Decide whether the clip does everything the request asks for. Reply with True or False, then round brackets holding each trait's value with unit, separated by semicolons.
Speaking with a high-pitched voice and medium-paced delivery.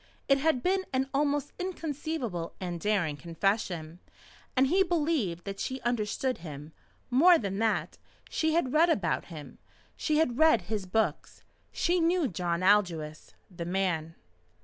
True (220 Hz; 145 wpm)